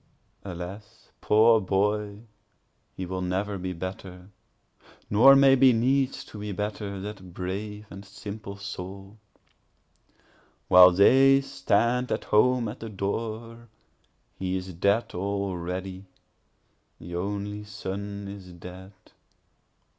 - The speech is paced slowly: Yes, slow, 105 wpm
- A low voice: Yes, low, 100 Hz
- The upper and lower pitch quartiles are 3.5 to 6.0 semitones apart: No, narrow, 2.5 semitones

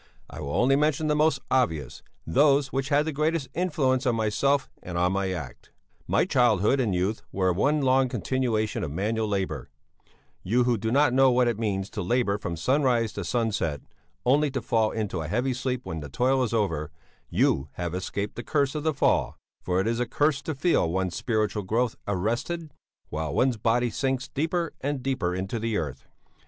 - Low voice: Yes, low, 120 Hz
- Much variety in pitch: Yes, wide, 5.8 semitones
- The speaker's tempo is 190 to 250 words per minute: Yes, average, 195 wpm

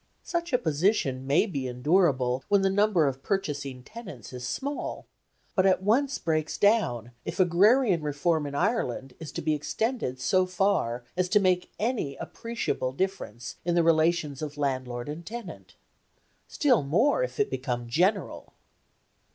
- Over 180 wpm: No, average, 150 wpm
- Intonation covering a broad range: Yes, wide, 7.1 semitones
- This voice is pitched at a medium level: Yes, medium, 165 Hz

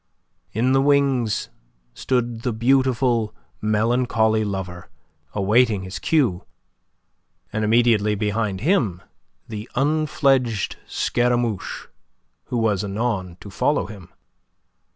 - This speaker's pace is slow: Yes, slow, 95 wpm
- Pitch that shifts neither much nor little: Yes, average, 3.4 semitones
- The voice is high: No, low, 115 Hz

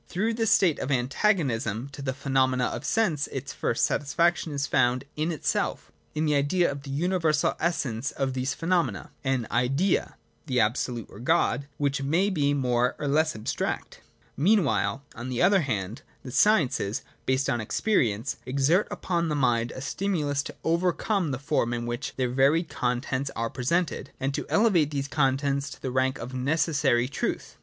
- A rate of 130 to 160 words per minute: No, average, 175 wpm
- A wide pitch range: No, average, 4.2 semitones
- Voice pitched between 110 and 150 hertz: Yes, medium, 140 Hz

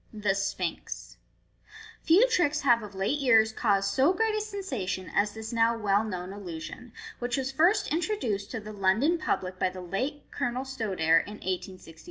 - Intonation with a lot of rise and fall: Yes, wide, 6.8 semitones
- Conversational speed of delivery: Yes, average, 175 wpm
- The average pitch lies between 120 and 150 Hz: No, high, 220 Hz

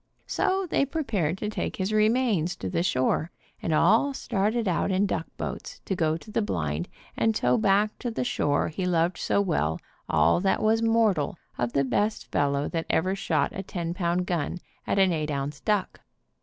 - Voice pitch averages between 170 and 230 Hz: Yes, medium, 185 Hz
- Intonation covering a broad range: Yes, wide, 5.7 semitones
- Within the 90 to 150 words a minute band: No, average, 195 wpm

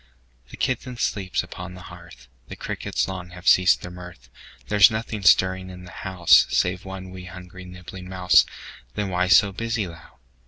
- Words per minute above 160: Yes, average, 170 wpm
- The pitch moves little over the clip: Yes, narrow, 1.1 semitones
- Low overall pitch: Yes, very low, 90 Hz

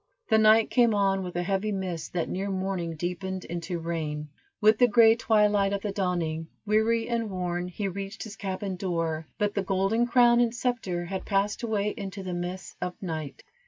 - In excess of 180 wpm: Yes, average, 190 wpm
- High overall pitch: Yes, high, 195 Hz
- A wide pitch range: No, average, 3.3 semitones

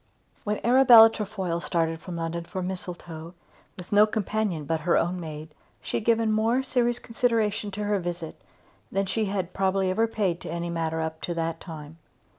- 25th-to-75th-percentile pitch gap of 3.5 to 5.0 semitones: Yes, average, 4.4 semitones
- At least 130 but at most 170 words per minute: No, average, 180 wpm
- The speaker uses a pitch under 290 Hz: Yes, medium, 185 Hz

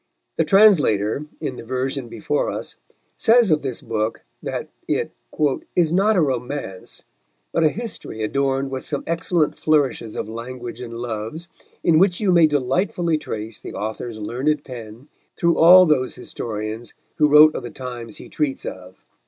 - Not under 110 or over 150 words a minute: No, average, 160 wpm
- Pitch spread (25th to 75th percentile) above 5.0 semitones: Yes, wide, 5.6 semitones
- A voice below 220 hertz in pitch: Yes, low, 135 Hz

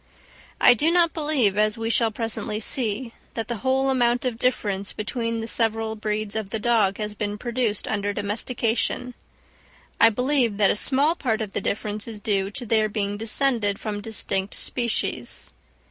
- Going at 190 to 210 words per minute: No, average, 170 wpm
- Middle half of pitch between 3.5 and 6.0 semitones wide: No, average, 2.8 semitones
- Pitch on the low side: No, high, 225 Hz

